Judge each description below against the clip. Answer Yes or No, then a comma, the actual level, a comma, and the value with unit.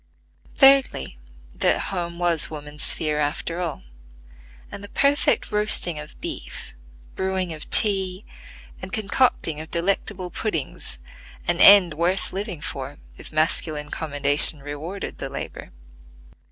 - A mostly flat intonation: No, average, 4.4 semitones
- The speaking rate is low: Yes, slow, 120 wpm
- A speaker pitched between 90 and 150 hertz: No, medium, 170 Hz